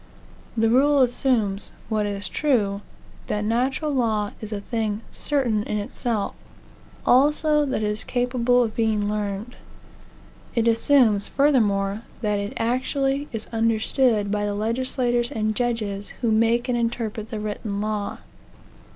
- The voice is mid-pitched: No, high, 225 Hz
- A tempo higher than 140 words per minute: No, slow, 135 wpm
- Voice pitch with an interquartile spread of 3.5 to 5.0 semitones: No, average, 3.0 semitones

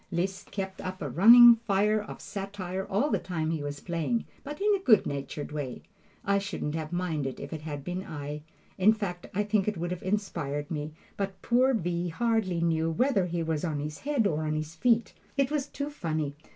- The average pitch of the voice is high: No, medium, 180 Hz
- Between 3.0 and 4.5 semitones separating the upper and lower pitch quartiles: No, average, 5.2 semitones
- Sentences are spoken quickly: Yes, fast, 210 wpm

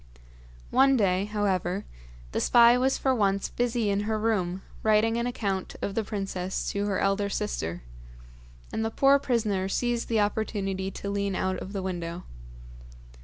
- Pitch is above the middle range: Yes, high, 205 Hz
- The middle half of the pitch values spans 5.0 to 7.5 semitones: No, average, 2.9 semitones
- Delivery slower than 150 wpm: No, average, 160 wpm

